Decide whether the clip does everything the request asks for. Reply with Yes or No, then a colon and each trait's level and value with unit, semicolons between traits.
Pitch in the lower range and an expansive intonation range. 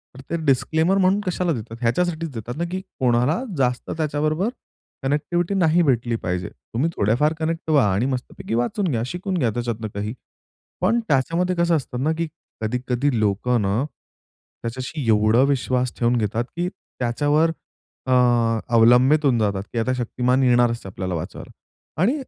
Yes: low, 130 Hz; wide, 5.8 semitones